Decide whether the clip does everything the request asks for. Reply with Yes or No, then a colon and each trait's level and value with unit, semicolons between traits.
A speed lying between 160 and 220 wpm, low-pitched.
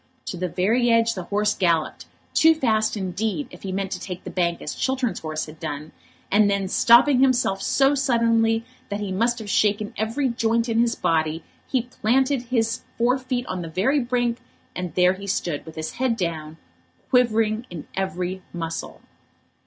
No: average, 180 wpm; high, 215 Hz